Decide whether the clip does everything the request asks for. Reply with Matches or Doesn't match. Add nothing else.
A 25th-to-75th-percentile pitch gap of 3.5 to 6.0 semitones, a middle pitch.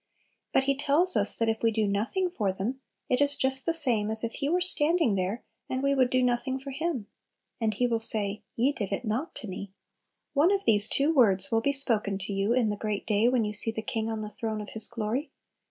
Doesn't match